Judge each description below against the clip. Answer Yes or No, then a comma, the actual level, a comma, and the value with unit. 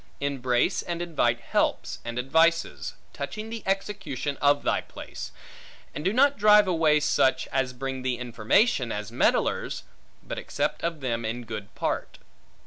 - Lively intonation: Yes, wide, 5.9 semitones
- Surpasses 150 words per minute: No, average, 145 wpm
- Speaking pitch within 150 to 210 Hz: No, medium, 140 Hz